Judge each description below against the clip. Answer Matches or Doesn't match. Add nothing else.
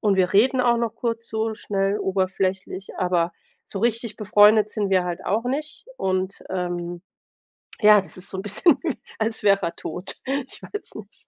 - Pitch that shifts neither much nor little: Matches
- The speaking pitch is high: Matches